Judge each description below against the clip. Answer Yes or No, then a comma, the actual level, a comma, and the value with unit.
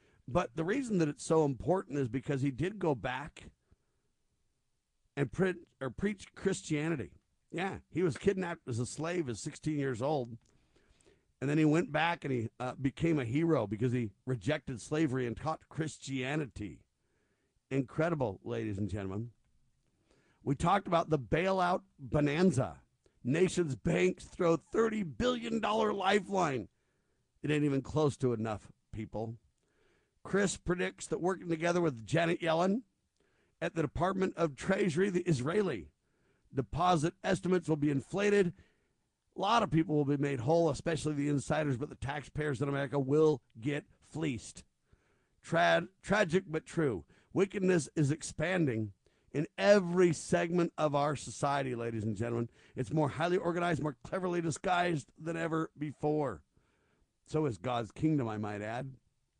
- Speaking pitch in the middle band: Yes, medium, 155 Hz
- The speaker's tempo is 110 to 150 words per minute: Yes, average, 145 wpm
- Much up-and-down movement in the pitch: No, average, 4.8 semitones